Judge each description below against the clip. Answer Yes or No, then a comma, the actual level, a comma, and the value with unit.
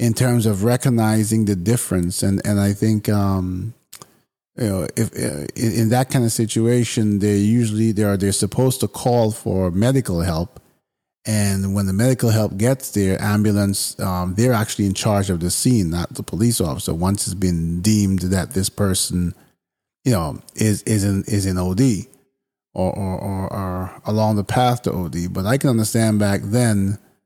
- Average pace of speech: Yes, average, 180 wpm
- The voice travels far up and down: No, average, 3.1 semitones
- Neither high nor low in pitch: No, low, 105 Hz